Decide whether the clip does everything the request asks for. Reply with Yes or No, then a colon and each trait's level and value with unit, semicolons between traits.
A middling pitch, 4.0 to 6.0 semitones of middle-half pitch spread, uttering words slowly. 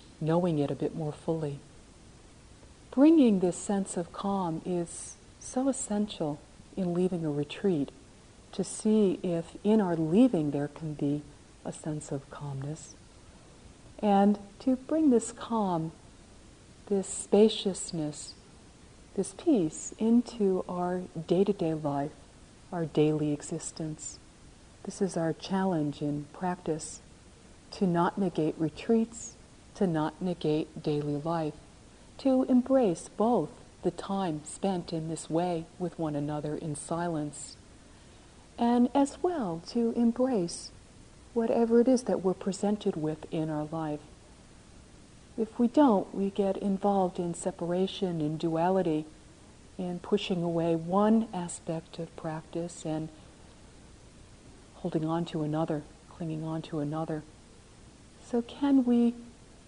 Yes: medium, 175 Hz; average, 4.6 semitones; slow, 125 wpm